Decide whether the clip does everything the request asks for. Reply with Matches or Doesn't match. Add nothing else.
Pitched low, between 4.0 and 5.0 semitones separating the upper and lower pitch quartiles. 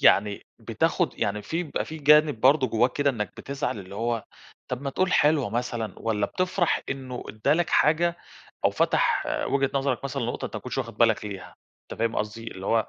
Matches